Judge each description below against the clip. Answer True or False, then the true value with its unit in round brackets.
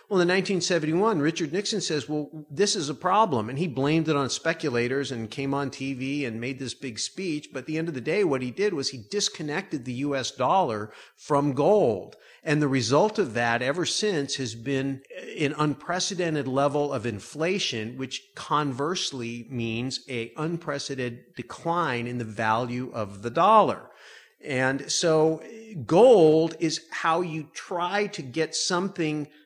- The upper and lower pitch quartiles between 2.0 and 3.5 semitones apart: False (4.1 semitones)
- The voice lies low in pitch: False (145 Hz)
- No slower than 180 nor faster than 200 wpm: False (165 wpm)